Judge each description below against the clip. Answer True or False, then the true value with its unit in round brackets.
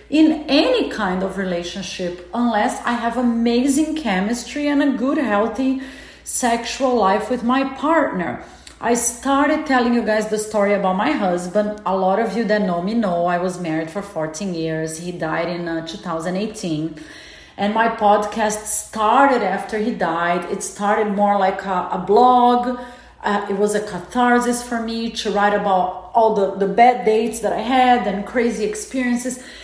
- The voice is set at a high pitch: True (215 Hz)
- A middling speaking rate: True (170 wpm)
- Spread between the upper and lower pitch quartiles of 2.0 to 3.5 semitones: False (4.3 semitones)